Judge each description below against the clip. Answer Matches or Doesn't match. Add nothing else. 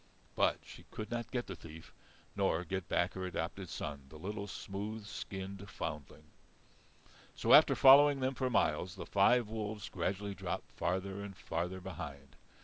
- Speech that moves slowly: Doesn't match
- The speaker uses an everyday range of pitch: Matches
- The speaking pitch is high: Doesn't match